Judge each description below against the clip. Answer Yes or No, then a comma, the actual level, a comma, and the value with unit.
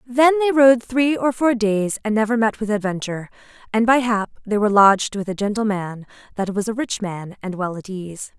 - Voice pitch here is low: No, high, 215 Hz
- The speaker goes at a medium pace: No, fast, 220 wpm